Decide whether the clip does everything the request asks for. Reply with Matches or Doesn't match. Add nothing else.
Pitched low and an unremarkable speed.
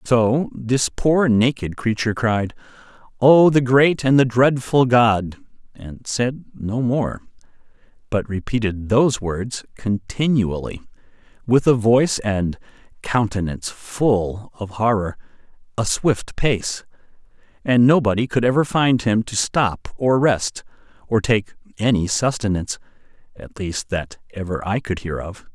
Doesn't match